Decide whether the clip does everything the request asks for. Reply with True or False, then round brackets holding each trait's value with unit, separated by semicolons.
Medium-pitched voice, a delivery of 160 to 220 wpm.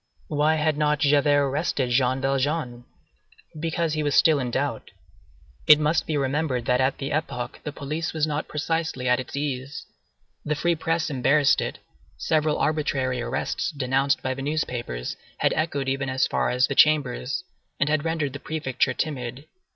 True (145 Hz; 165 wpm)